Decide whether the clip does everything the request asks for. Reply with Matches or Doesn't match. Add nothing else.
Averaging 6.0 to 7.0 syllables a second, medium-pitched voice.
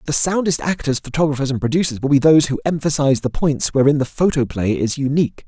Matches